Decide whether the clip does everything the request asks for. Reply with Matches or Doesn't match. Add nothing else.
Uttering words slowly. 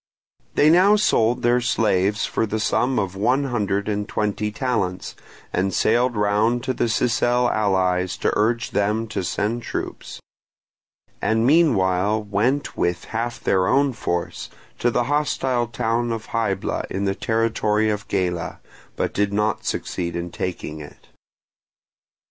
Doesn't match